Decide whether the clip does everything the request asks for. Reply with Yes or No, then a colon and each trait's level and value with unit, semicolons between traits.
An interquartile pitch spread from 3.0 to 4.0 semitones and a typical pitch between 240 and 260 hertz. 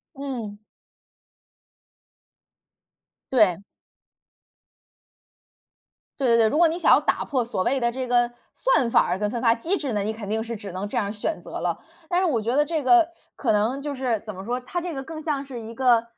No: average, 4.4 semitones; high, 245 Hz